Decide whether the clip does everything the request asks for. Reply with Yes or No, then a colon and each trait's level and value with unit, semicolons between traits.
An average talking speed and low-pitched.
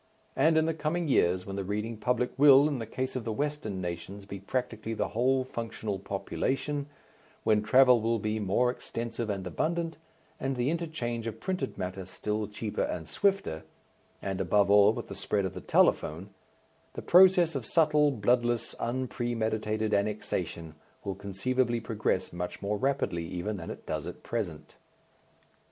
Yes: average, 165 wpm; low, 115 Hz